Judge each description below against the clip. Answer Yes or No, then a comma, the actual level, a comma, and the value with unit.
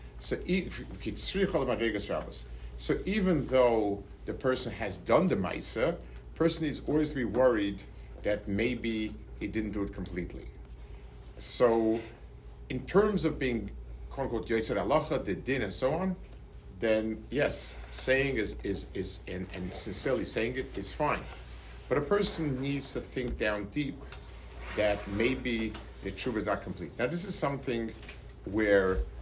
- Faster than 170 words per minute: No, average, 140 wpm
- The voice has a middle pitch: No, low, 110 Hz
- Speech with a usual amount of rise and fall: No, wide, 6.3 semitones